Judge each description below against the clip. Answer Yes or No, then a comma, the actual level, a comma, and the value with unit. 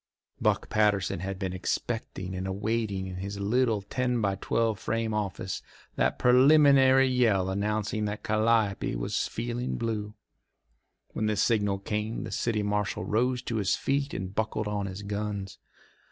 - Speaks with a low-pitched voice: Yes, low, 105 Hz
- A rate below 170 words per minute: Yes, average, 150 wpm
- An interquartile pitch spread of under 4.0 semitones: Yes, average, 2.8 semitones